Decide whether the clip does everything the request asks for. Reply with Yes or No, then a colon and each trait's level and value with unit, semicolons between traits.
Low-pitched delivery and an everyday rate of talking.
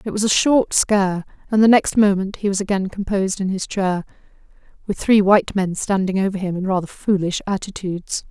No: high, 195 Hz; average, 195 wpm